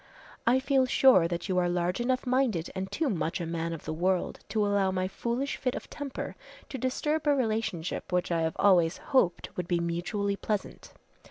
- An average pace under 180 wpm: No, average, 195 wpm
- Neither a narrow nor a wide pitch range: No, wide, 6.7 semitones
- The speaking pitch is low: No, high, 195 Hz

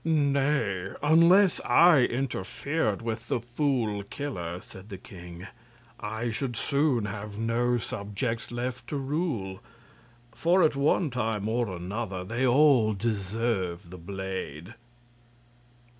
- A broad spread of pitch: Yes, wide, 5.7 semitones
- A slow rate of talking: Yes, slow, 115 wpm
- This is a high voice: No, low, 115 Hz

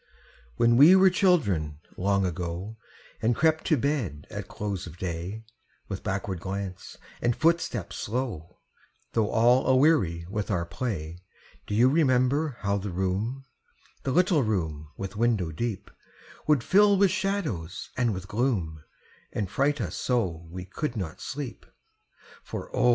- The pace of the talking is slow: No, average, 145 wpm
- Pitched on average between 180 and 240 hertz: No, low, 110 Hz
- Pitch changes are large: Yes, wide, 6.7 semitones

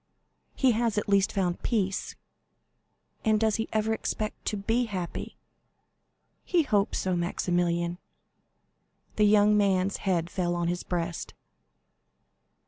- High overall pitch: Yes, high, 200 Hz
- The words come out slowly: Yes, slow, 125 wpm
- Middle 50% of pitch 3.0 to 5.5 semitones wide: Yes, average, 3.4 semitones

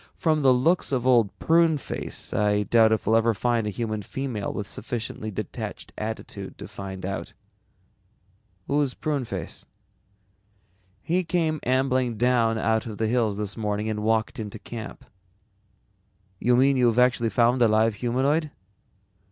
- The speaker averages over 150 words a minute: No, average, 145 wpm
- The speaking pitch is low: Yes, low, 115 Hz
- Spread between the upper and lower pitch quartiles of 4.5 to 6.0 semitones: No, average, 3.2 semitones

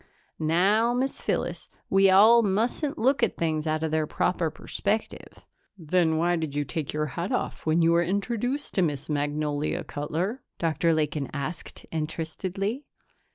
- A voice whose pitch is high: No, medium, 170 Hz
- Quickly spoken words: No, average, 155 wpm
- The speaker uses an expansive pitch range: No, average, 4.7 semitones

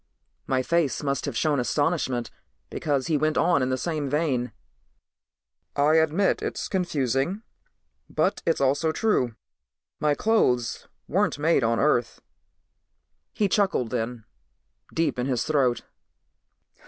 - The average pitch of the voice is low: No, medium, 145 Hz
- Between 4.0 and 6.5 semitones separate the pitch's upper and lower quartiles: Yes, average, 4.3 semitones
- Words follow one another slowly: Yes, slow, 125 wpm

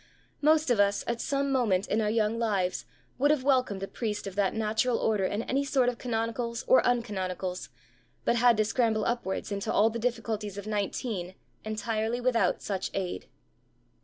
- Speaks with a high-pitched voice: Yes, high, 220 Hz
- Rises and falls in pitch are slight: No, average, 3.2 semitones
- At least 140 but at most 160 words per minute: No, average, 175 wpm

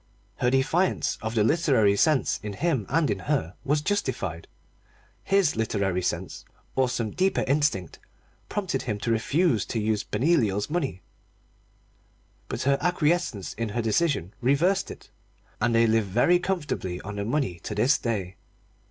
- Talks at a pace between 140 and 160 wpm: Yes, average, 150 wpm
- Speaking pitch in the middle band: No, low, 120 Hz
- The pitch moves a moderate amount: No, wide, 7.0 semitones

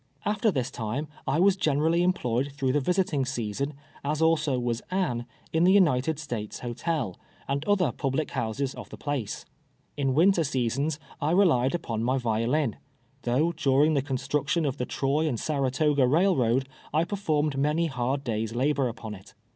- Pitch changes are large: No, average, 4.2 semitones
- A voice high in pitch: No, medium, 140 Hz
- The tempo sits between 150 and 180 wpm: Yes, average, 165 wpm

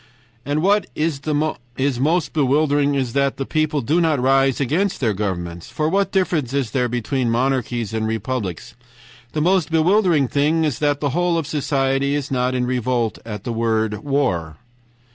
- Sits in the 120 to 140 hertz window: Yes, low, 135 Hz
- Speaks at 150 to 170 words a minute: Yes, average, 165 wpm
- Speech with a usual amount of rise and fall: Yes, average, 4.3 semitones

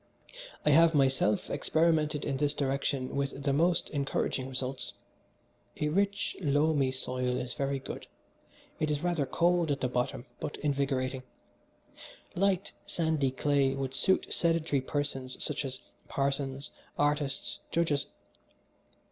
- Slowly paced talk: Yes, slow, 125 wpm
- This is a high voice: No, medium, 140 Hz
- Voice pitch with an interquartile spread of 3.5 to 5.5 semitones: No, narrow, 2.6 semitones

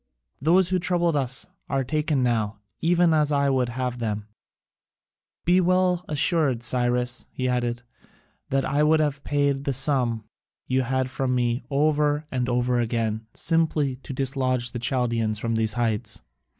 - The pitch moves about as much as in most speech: Yes, average, 3.7 semitones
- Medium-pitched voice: No, low, 130 Hz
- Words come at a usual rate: Yes, average, 150 wpm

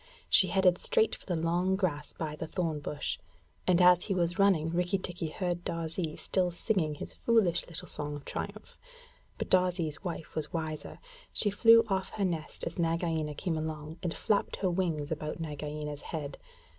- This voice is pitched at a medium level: Yes, medium, 170 Hz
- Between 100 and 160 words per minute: No, average, 175 wpm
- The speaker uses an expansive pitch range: No, average, 3.1 semitones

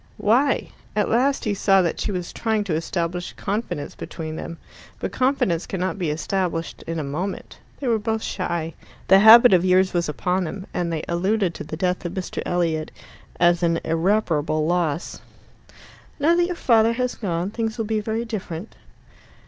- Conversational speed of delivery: Yes, average, 175 wpm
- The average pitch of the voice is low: No, medium, 185 Hz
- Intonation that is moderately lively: Yes, average, 4.7 semitones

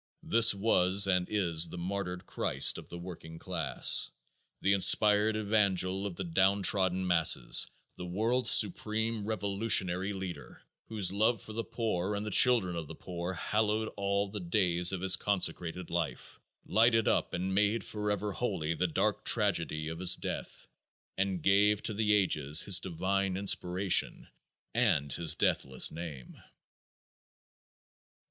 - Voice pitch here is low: Yes, very low, 95 Hz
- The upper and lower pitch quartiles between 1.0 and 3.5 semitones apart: Yes, average, 3.0 semitones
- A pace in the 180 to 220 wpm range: No, average, 140 wpm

